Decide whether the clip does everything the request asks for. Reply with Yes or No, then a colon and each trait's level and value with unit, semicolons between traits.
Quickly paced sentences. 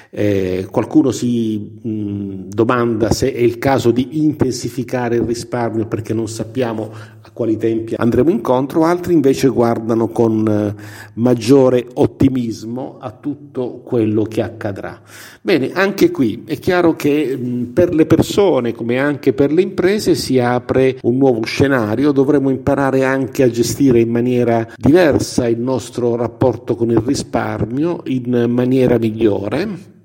No: average, 140 wpm